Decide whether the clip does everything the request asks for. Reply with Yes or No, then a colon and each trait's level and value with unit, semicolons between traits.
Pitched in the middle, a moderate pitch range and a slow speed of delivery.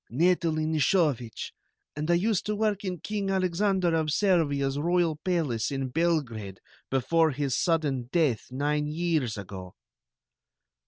Yes: medium, 155 Hz; average, 4.7 semitones; slow, 125 wpm